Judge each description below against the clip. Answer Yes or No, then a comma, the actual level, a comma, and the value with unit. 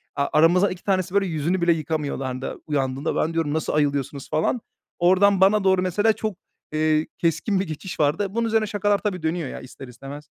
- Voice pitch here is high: No, medium, 165 Hz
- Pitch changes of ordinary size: Yes, average, 4.6 semitones